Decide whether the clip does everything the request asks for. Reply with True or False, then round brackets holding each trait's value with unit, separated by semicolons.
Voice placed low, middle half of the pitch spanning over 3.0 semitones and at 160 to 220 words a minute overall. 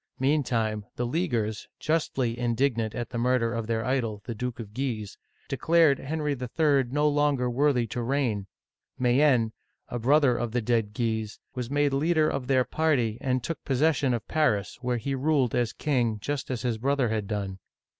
True (125 Hz; 3.6 semitones; 180 wpm)